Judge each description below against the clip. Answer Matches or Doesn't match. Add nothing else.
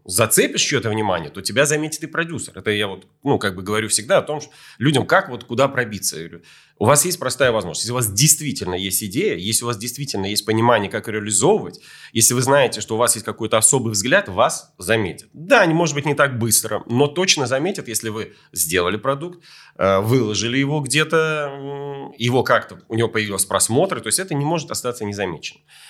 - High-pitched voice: Doesn't match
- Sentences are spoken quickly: Matches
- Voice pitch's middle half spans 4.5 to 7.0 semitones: Matches